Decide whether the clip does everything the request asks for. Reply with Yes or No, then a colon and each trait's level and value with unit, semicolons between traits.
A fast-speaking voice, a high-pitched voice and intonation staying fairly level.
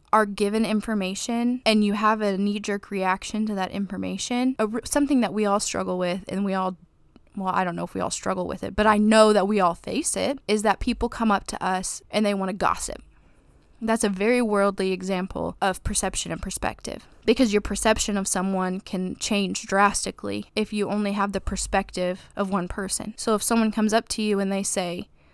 Yes: fast, 210 wpm; high, 205 Hz; narrow, 2.3 semitones